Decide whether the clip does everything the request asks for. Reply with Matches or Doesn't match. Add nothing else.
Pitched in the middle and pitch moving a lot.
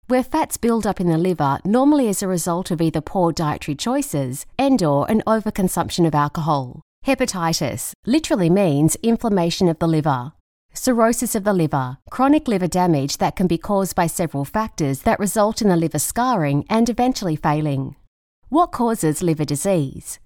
Matches